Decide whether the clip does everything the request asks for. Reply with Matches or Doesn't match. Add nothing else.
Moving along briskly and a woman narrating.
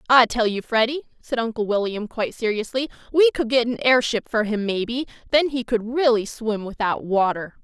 Doesn't match